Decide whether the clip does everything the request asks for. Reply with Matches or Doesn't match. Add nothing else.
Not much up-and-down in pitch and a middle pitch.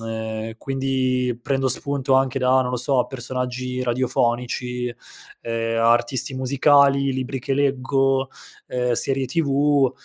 Doesn't match